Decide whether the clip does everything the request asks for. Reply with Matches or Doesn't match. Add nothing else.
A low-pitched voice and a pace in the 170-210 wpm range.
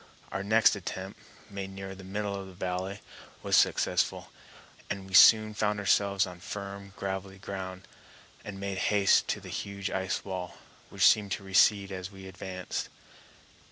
Doesn't match